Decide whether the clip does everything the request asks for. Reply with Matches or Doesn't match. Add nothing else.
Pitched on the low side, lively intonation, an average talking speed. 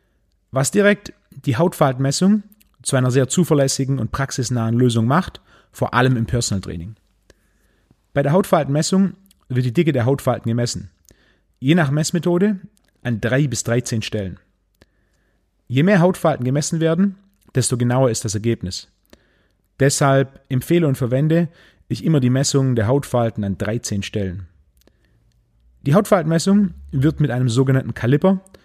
Matches